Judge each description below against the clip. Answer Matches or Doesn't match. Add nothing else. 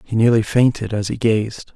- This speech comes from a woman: Doesn't match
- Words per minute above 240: Doesn't match